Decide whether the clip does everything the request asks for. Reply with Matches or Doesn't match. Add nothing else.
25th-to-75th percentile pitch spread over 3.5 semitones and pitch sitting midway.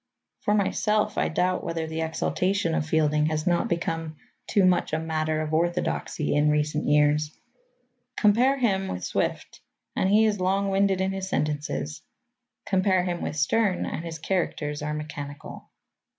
Matches